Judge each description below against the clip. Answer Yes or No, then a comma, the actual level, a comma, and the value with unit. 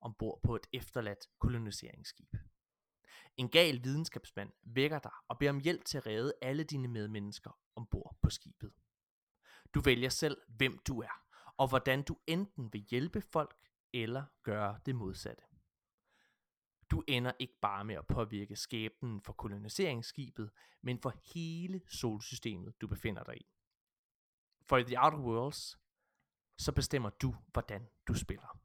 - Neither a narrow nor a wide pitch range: Yes, average, 4.3 semitones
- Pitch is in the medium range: No, low, 125 Hz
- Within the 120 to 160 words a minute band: Yes, slow, 145 wpm